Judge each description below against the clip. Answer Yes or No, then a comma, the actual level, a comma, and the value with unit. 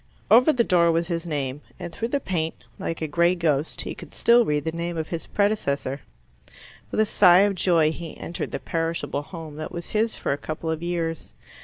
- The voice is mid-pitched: Yes, medium, 170 Hz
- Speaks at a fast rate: Yes, fast, 210 wpm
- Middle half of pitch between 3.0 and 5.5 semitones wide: No, narrow, 2.6 semitones